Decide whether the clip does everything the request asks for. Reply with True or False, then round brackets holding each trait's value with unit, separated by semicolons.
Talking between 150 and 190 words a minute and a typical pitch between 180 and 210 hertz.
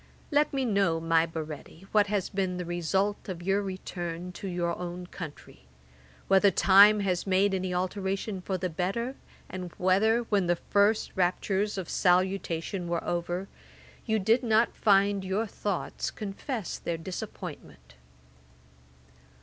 False (140 wpm; 190 Hz)